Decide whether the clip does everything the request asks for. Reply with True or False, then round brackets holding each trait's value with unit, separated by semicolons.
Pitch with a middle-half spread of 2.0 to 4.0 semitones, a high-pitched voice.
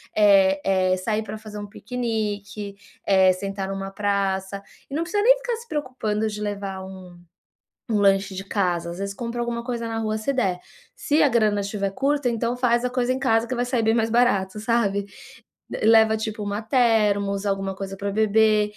True (3.1 semitones; 210 Hz)